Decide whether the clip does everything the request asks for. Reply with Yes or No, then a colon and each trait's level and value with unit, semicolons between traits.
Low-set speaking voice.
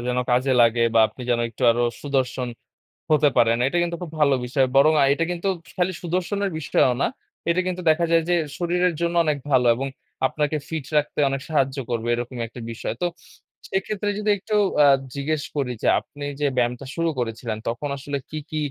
No: medium, 145 Hz